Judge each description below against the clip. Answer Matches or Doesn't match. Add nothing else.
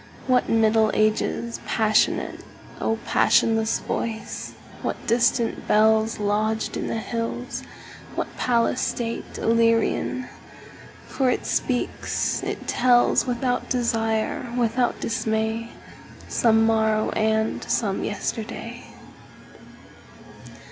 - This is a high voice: Matches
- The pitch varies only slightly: Matches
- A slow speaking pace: Matches